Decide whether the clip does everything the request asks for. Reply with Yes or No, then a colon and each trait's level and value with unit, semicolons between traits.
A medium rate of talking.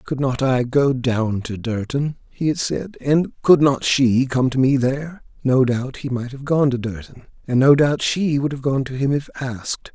No: fast, 225 wpm